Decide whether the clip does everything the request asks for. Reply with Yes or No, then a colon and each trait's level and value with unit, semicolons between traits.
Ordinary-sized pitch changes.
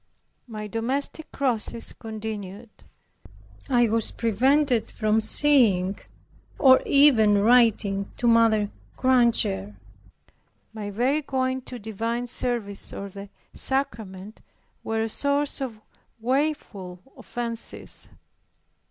Yes: average, 3.7 semitones